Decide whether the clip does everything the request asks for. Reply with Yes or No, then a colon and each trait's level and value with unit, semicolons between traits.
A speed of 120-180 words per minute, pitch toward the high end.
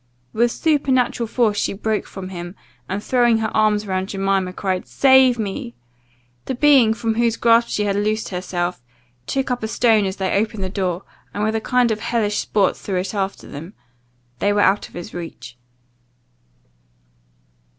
Yes: average, 170 wpm; high, 210 Hz